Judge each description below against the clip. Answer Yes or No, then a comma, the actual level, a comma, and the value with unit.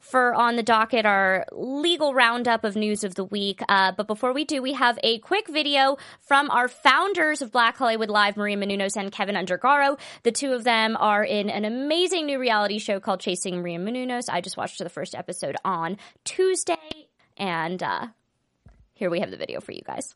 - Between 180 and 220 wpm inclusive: Yes, average, 200 wpm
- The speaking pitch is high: Yes, high, 230 Hz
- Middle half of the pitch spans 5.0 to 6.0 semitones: Yes, wide, 5.4 semitones